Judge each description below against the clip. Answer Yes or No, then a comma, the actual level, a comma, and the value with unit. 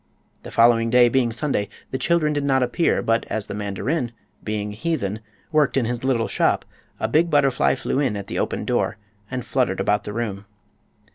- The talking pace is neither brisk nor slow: Yes, average, 195 wpm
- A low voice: Yes, low, 120 Hz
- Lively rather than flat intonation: No, average, 4.5 semitones